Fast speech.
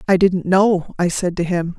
Yes: fast, 235 wpm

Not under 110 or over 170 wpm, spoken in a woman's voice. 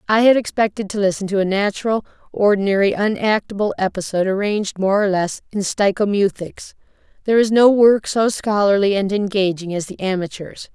Yes: average, 155 wpm; female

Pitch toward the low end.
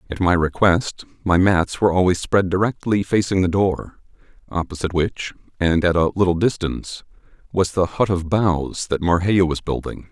Yes: very low, 90 Hz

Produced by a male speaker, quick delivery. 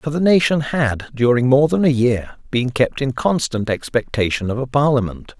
No: male; average, 190 wpm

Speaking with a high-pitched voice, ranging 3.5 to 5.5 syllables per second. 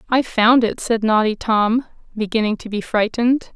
Yes: high, 225 Hz; 4.9 syllables/s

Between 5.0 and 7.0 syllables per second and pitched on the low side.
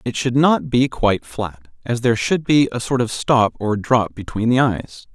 No: 4.6 syllables/s; low, 120 Hz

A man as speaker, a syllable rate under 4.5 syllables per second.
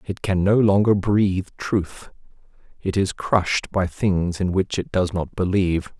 Yes: male; 4.3 syllables/s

